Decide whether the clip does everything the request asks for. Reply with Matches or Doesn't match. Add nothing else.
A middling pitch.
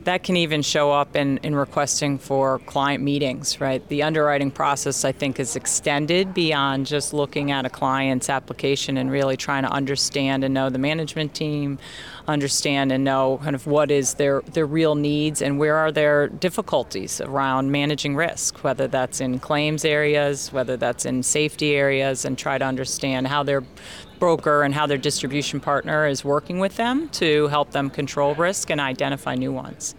Matches